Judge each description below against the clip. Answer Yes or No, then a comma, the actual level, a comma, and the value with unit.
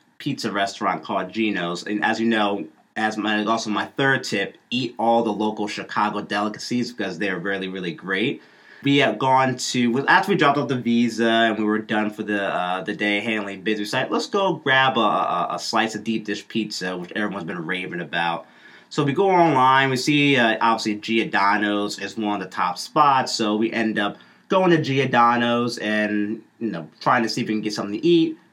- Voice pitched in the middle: No, low, 110 Hz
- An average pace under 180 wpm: No, fast, 205 wpm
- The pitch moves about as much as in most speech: Yes, average, 3.0 semitones